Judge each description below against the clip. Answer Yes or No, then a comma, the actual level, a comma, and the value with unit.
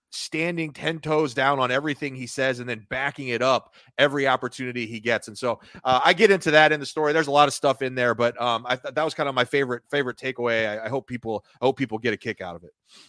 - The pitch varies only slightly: No, average, 3.2 semitones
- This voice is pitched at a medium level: No, low, 130 Hz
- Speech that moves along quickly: Yes, fast, 270 wpm